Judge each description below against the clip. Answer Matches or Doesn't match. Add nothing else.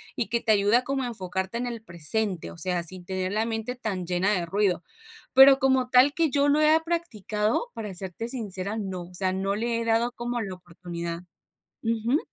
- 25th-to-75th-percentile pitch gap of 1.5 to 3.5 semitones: Doesn't match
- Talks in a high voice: Matches